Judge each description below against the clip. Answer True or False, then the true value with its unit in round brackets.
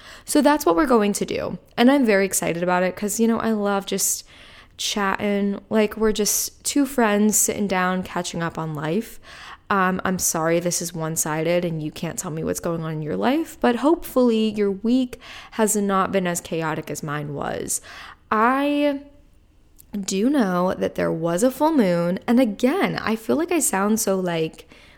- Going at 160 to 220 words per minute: True (190 wpm)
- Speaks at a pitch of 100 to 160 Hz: False (200 Hz)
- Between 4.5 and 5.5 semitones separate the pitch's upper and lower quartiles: True (5.0 semitones)